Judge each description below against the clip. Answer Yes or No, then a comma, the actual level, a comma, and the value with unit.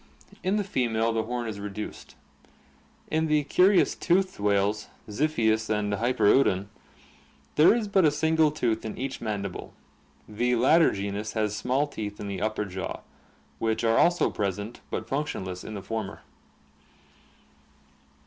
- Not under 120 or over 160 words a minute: Yes, average, 145 wpm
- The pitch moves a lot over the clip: Yes, wide, 6.3 semitones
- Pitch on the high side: No, low, 110 Hz